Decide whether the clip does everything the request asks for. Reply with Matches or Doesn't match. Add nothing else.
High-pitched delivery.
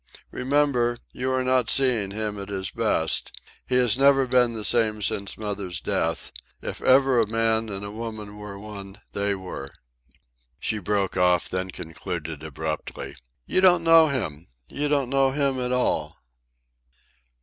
Doesn't match